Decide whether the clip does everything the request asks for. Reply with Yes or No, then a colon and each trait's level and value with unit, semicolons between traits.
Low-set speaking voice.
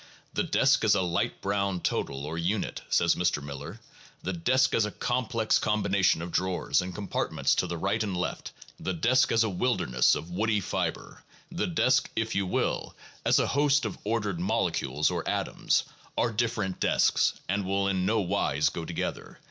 Yes: low, 100 Hz